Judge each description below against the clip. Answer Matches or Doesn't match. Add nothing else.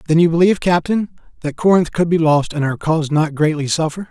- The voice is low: Doesn't match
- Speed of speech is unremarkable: Doesn't match